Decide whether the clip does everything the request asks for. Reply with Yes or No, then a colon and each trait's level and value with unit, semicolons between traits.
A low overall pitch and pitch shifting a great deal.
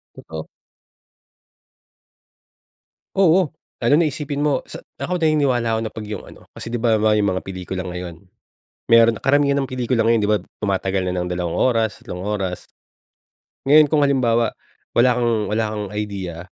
Yes: low, 115 Hz; wide, 5.9 semitones